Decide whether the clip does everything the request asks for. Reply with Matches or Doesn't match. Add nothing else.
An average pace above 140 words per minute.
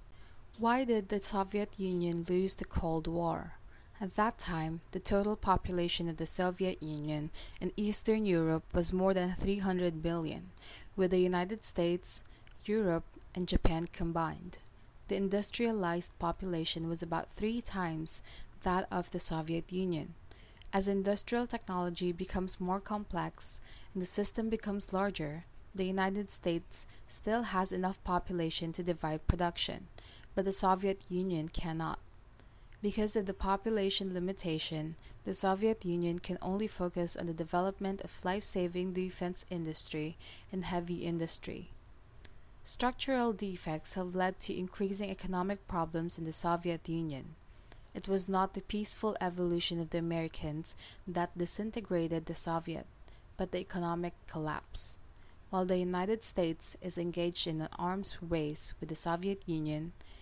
Doesn't match